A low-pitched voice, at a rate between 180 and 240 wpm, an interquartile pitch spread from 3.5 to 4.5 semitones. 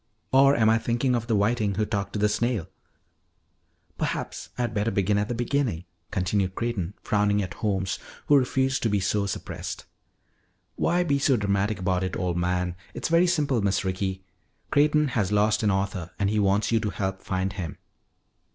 Yes: low, 105 Hz; average, 185 wpm; average, 3.8 semitones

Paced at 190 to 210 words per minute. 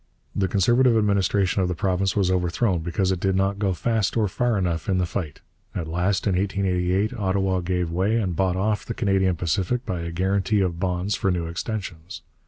Yes: average, 195 wpm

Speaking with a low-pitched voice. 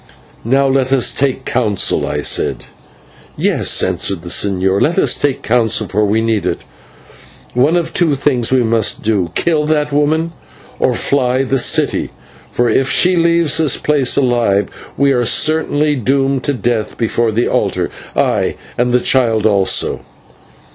Yes: low, 130 Hz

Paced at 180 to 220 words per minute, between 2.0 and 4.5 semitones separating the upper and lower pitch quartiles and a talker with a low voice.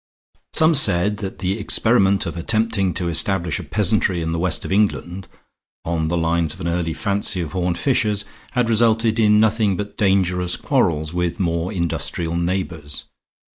No: average, 165 wpm; average, 3.6 semitones; very low, 95 Hz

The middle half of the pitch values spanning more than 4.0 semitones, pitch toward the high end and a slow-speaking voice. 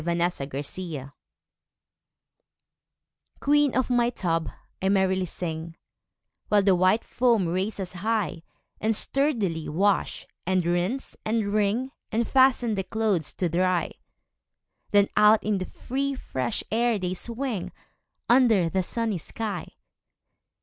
Yes: average, 4.5 semitones; high, 200 Hz; slow, 120 wpm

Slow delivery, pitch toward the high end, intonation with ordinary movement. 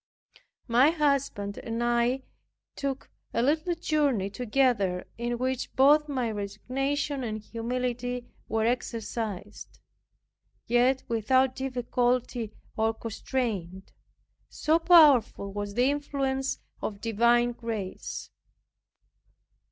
Yes: slow, 95 wpm; high, 245 Hz; average, 3.2 semitones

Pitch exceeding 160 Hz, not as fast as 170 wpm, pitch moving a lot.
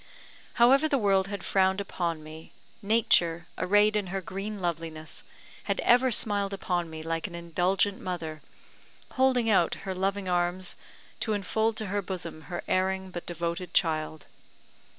No: high, 190 Hz; average, 150 wpm; average, 3.1 semitones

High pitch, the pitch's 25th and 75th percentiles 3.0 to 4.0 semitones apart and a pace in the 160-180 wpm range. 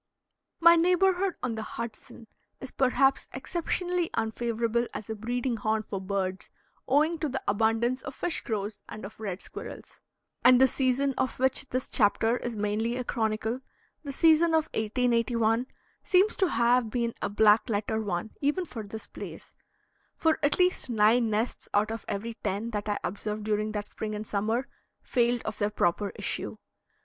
Yes: high, 230 Hz; average, 3.7 semitones; average, 165 wpm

